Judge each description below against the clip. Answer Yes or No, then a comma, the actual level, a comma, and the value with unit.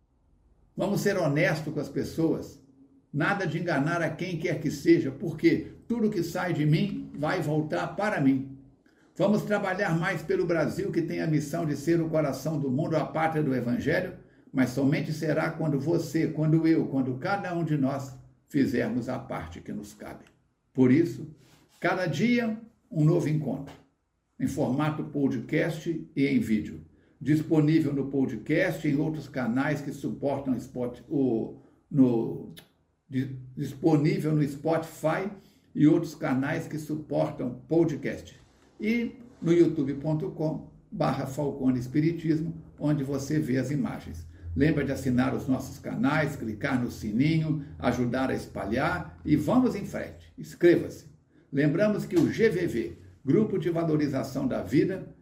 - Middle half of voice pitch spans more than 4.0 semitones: No, average, 3.6 semitones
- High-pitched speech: No, medium, 150 Hz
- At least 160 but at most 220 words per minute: No, average, 140 wpm